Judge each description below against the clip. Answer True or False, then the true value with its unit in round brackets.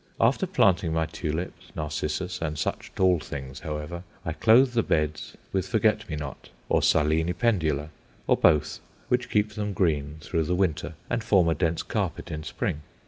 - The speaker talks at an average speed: True (170 wpm)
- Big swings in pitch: False (4.3 semitones)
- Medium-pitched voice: False (85 Hz)